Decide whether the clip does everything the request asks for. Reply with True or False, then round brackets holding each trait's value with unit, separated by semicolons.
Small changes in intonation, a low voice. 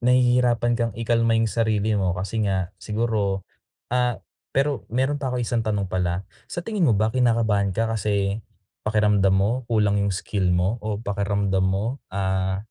False (3.2 semitones; 110 Hz)